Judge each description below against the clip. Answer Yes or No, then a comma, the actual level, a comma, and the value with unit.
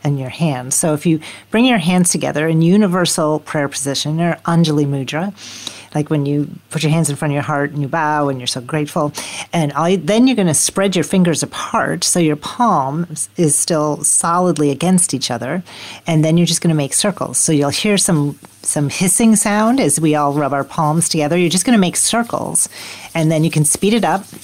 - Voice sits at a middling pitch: Yes, medium, 160 Hz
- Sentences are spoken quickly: Yes, fast, 220 wpm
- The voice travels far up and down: No, average, 3.5 semitones